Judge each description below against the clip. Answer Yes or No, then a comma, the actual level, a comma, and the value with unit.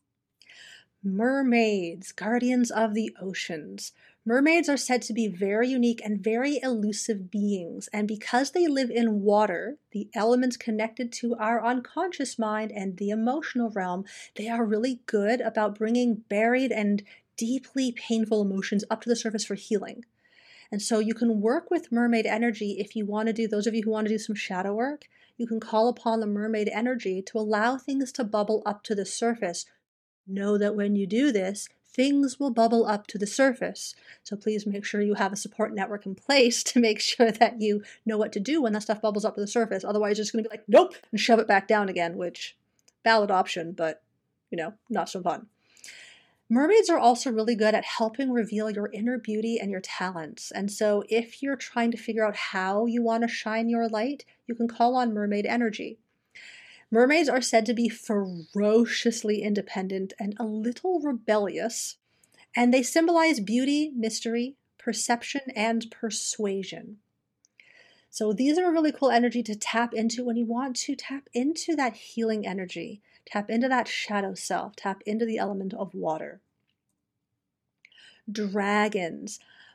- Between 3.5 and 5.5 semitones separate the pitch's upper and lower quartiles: No, narrow, 2.6 semitones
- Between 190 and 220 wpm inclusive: No, average, 180 wpm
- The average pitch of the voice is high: Yes, high, 225 Hz